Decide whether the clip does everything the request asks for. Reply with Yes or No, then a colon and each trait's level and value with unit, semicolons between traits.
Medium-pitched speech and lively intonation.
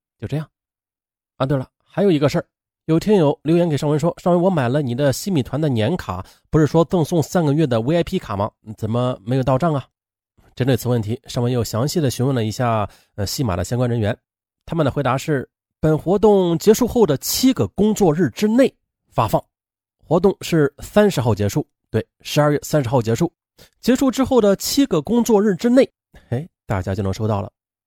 Yes: medium, 145 Hz; wide, 7.1 semitones